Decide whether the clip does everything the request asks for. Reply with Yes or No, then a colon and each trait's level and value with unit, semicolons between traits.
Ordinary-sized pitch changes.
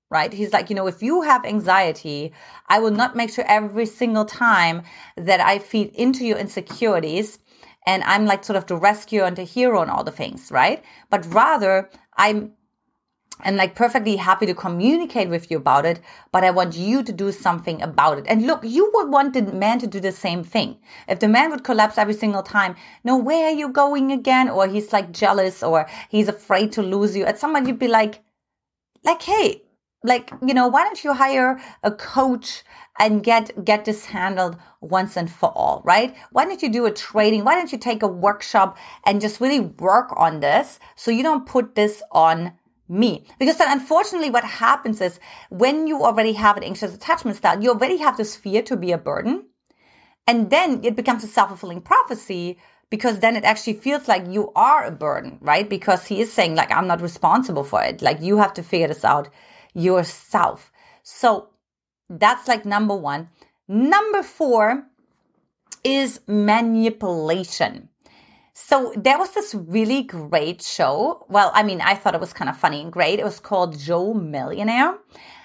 Yes: average, 4.8 semitones